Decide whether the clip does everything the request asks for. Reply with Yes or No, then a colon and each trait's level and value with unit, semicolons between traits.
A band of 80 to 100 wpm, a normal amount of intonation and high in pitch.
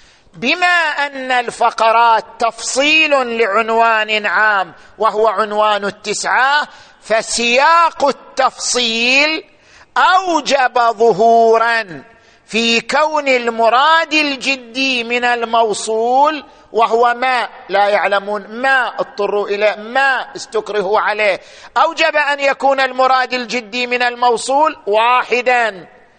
Yes: average, 85 wpm; average, 3.4 semitones; high, 240 Hz